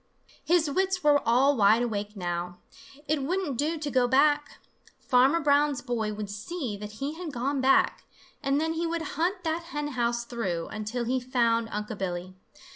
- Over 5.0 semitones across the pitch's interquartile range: Yes, wide, 5.5 semitones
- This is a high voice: Yes, very high, 260 Hz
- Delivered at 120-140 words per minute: No, average, 175 wpm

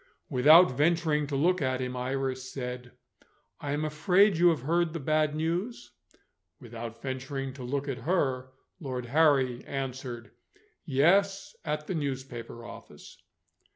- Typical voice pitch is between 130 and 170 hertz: Yes, medium, 140 Hz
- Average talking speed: No, slow, 130 wpm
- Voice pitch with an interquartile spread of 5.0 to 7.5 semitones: No, average, 3.9 semitones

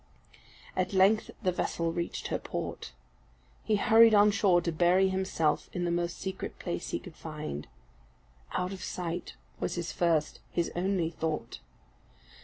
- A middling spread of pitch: No, narrow, 2.3 semitones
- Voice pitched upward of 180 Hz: No, medium, 175 Hz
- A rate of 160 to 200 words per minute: No, average, 150 wpm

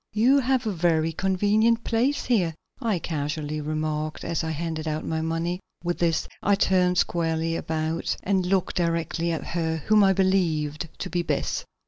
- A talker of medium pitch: Yes, medium, 170 Hz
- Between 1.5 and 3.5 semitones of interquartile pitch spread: Yes, average, 3.2 semitones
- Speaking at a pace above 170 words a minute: No, average, 165 wpm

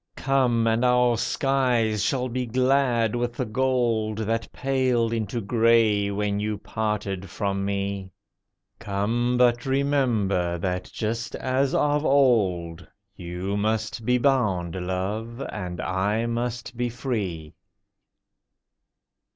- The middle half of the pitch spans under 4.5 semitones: Yes, average, 3.7 semitones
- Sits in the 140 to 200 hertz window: No, low, 115 Hz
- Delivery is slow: Yes, slow, 115 wpm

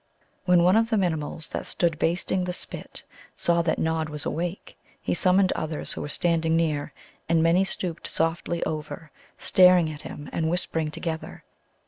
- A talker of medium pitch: Yes, medium, 165 Hz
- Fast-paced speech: No, average, 165 wpm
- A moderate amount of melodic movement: No, narrow, 2.1 semitones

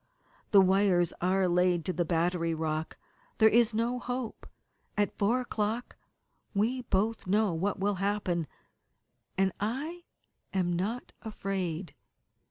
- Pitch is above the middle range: Yes, high, 195 Hz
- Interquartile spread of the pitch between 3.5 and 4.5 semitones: Yes, average, 3.8 semitones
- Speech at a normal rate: No, slow, 125 wpm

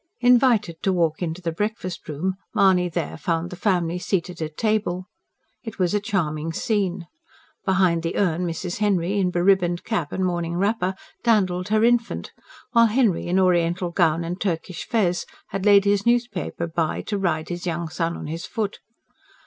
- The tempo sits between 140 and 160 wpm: No, average, 175 wpm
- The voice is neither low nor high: Yes, medium, 180 Hz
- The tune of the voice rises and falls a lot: No, average, 3.2 semitones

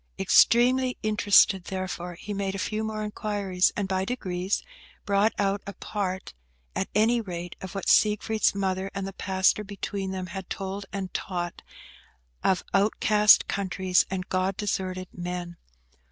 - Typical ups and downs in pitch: No, narrow, 1.9 semitones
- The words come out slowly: No, average, 145 wpm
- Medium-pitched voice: No, high, 195 Hz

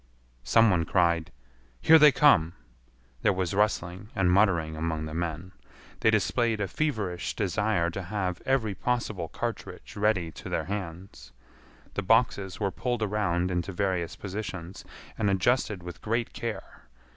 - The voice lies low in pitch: Yes, very low, 95 Hz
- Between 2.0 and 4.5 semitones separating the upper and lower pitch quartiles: Yes, average, 3.8 semitones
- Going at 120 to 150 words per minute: Yes, average, 145 wpm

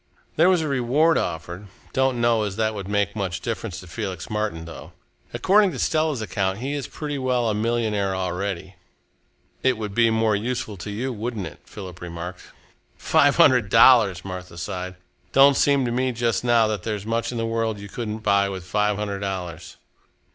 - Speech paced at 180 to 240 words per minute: Yes, average, 185 wpm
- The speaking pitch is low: Yes, low, 110 Hz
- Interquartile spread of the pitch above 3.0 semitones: Yes, average, 4.0 semitones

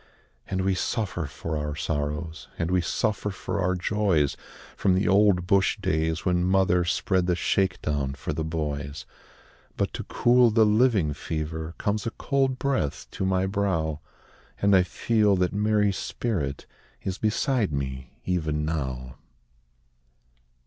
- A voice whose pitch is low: Yes, very low, 90 Hz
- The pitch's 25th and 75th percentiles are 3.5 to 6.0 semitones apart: Yes, average, 4.7 semitones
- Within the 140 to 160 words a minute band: Yes, average, 145 wpm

